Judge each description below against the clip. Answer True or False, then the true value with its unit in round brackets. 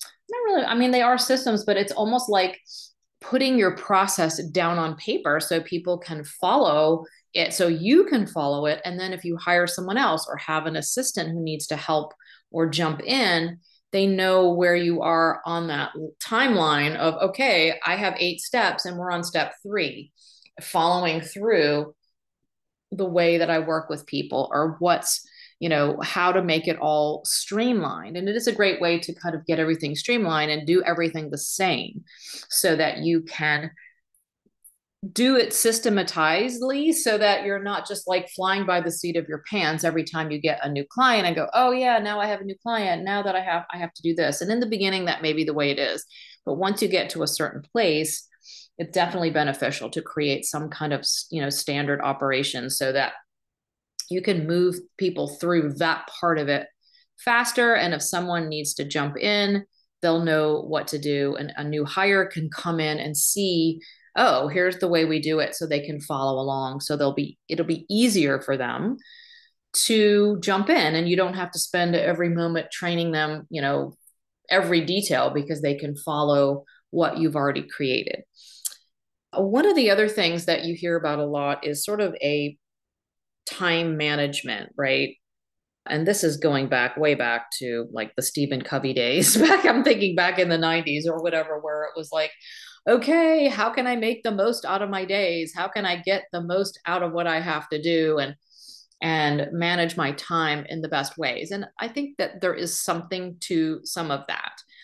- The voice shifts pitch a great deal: False (4.3 semitones)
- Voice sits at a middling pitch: True (170 Hz)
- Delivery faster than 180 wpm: True (195 wpm)